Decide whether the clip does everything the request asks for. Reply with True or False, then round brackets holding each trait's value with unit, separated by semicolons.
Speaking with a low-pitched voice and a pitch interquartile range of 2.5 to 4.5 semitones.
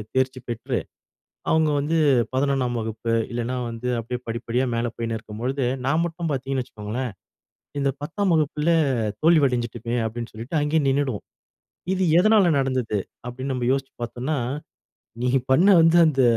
True (130 Hz; 3.8 semitones)